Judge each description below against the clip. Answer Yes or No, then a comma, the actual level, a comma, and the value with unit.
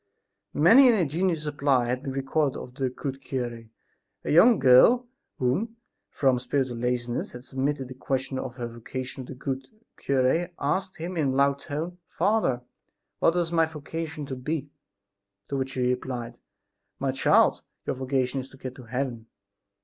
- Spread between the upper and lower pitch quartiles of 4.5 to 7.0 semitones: No, average, 3.8 semitones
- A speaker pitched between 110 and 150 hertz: Yes, low, 135 Hz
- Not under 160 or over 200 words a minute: Yes, average, 165 wpm